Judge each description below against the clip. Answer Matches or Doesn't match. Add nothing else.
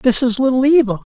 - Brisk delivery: Matches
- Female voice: Doesn't match